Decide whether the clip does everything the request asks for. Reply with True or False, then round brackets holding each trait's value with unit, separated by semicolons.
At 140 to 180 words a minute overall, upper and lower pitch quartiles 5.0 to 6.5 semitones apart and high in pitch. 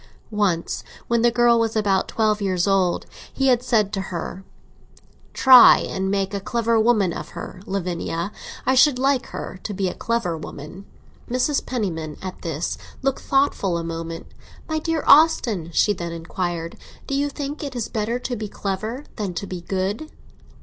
True (170 wpm; 5.3 semitones; 205 Hz)